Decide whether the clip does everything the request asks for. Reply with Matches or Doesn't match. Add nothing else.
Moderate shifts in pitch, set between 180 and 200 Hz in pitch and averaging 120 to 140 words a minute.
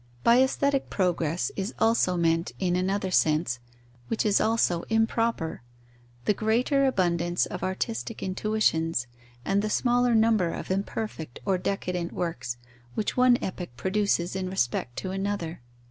Matches